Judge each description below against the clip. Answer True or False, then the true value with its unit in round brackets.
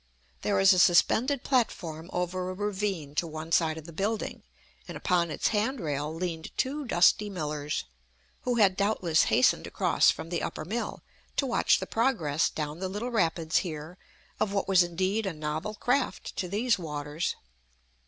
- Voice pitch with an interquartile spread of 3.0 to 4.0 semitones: False (4.7 semitones)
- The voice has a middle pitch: True (180 Hz)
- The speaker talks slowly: False (165 wpm)